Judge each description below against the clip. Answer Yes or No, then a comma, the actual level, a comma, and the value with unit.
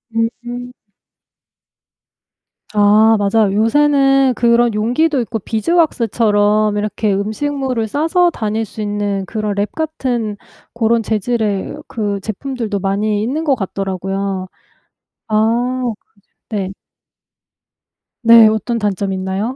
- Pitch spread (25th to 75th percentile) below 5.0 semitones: Yes, average, 3.0 semitones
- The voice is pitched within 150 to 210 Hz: No, high, 220 Hz